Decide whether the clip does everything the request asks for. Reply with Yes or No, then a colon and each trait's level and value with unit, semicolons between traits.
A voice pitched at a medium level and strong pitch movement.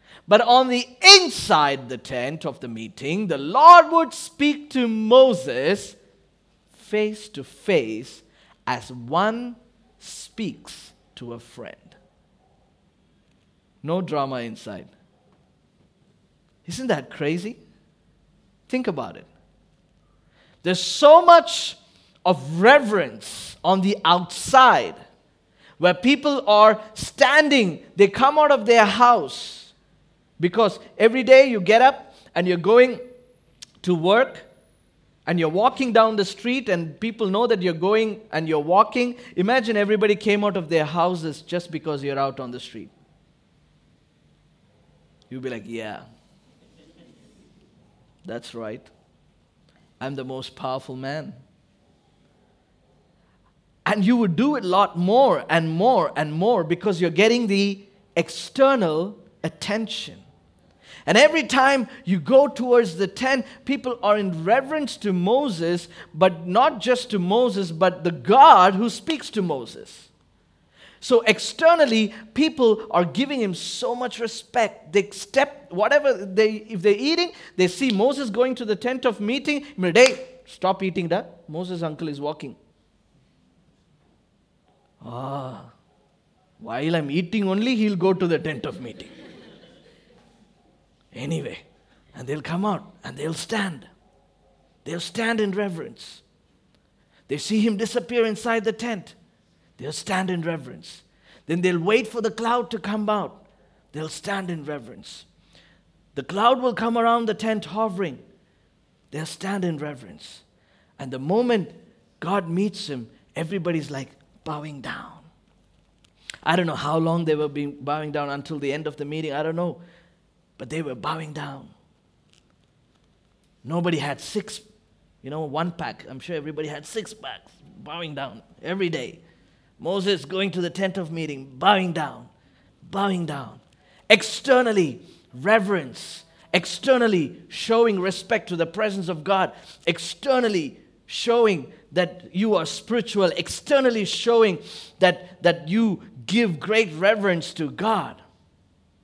No: high, 195 Hz; wide, 6.1 semitones